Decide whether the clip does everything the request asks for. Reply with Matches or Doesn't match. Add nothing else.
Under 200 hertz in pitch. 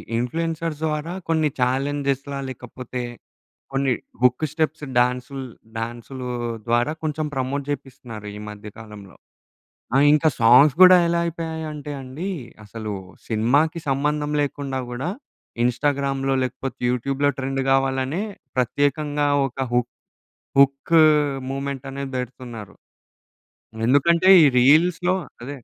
Matches